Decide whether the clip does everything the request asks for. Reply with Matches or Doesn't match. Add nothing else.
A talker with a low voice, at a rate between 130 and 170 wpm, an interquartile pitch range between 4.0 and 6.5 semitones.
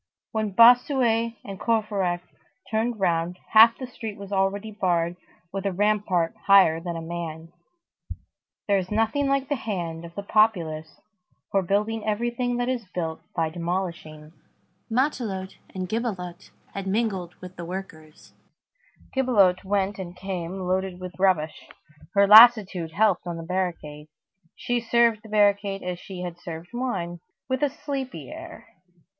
Doesn't match